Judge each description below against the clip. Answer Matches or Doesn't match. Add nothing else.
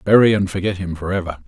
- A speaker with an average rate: Doesn't match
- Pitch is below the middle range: Matches